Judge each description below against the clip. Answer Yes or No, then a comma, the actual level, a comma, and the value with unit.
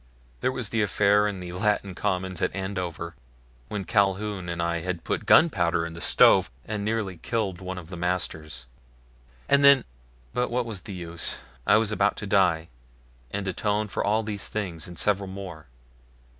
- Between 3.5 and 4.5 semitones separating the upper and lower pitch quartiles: No, average, 3.1 semitones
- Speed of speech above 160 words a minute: Yes, average, 175 wpm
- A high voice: No, very low, 95 Hz